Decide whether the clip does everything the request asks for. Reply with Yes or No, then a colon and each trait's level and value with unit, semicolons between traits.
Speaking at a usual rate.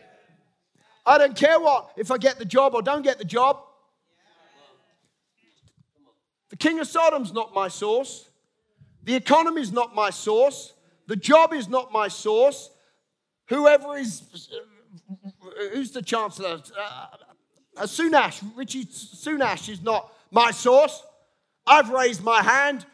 No: slow, 130 wpm